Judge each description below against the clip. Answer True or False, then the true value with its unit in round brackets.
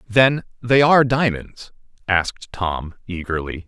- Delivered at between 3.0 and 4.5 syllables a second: True (4.2 syllables/s)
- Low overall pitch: True (110 Hz)